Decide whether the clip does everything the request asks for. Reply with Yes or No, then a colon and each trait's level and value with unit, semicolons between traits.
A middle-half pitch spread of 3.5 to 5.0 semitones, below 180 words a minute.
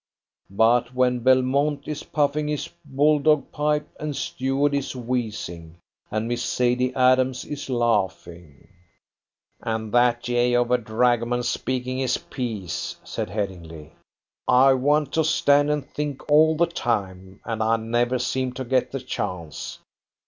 Yes: average, 3.8 semitones; average, 140 wpm